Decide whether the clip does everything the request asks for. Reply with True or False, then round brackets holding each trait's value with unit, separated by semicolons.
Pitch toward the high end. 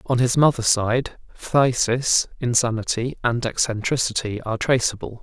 False (120 Hz)